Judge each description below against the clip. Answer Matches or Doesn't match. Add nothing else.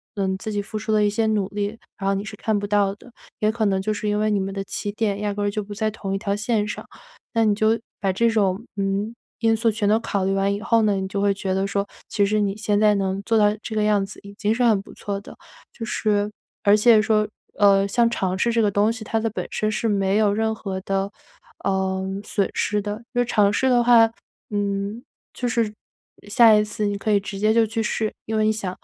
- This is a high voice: Matches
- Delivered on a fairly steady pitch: Matches